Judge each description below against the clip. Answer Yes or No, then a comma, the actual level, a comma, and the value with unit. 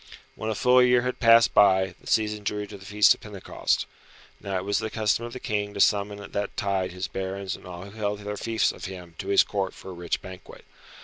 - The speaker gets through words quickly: Yes, fast, 245 wpm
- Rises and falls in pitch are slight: Yes, narrow, 2.1 semitones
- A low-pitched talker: Yes, low, 100 Hz